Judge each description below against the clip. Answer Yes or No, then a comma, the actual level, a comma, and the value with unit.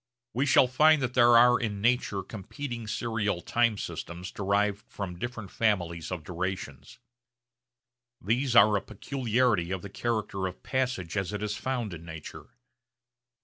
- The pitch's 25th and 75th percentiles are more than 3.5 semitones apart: Yes, average, 4.3 semitones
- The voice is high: No, low, 105 Hz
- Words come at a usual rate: Yes, average, 145 wpm